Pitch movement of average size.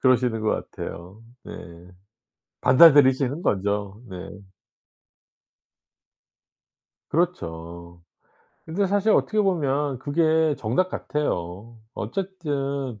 No: wide, 7.6 semitones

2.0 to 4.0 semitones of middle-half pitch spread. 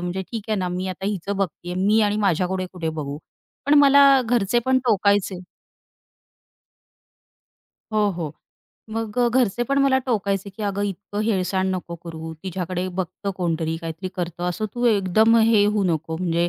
Yes: average, 3.5 semitones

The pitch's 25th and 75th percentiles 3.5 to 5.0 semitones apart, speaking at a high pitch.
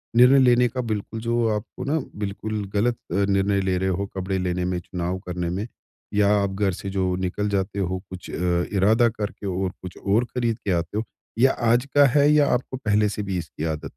No: average, 3.9 semitones; low, 100 Hz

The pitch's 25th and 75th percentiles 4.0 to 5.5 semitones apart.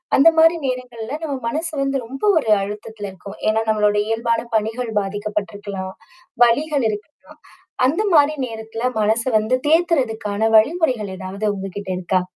Yes: average, 4.8 semitones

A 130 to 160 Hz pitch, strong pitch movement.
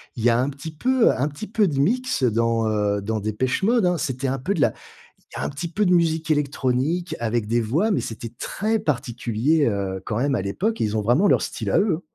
Yes: low, 135 Hz; wide, 7.1 semitones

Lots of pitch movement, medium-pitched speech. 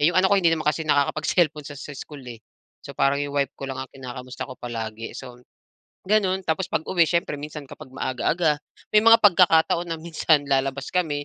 No: average, 3.9 semitones; medium, 150 Hz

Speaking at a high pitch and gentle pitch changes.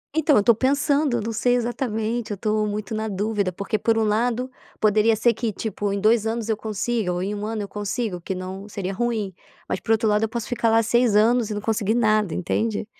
Yes: high, 220 Hz; narrow, 2.1 semitones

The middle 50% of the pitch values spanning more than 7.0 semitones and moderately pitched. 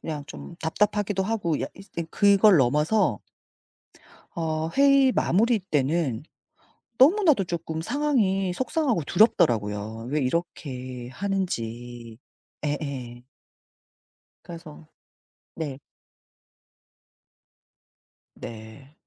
Yes: wide, 7.8 semitones; medium, 165 Hz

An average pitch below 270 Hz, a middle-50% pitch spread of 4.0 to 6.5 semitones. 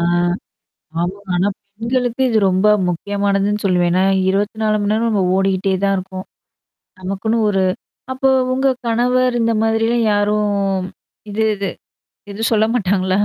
No: high, 205 Hz; average, 2.9 semitones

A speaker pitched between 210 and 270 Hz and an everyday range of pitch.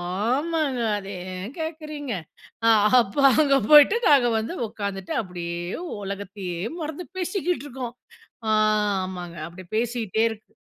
No: high, 230 Hz; wide, 7.4 semitones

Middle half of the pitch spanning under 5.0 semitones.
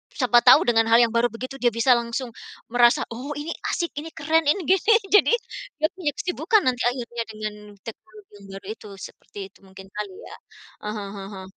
No: wide, 5.5 semitones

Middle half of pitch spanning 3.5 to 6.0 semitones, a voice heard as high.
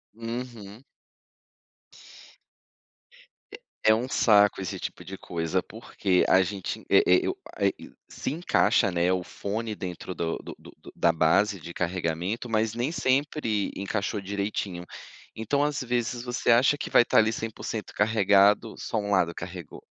No: average, 3.9 semitones; low, 105 Hz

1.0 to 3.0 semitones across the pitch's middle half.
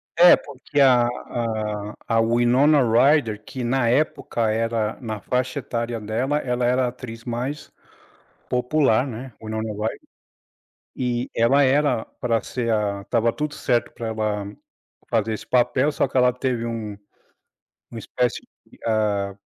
Yes: narrow, 2.5 semitones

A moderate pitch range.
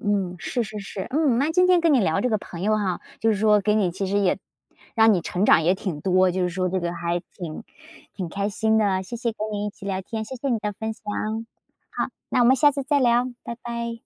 Yes: average, 4.0 semitones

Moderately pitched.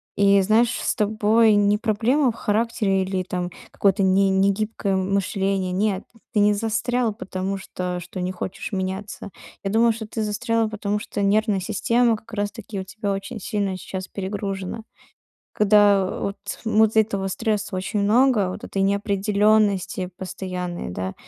No: high, 200 Hz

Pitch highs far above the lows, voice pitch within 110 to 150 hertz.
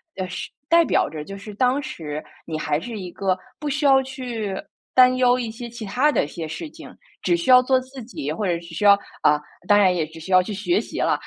No: wide, 6.5 semitones; high, 210 Hz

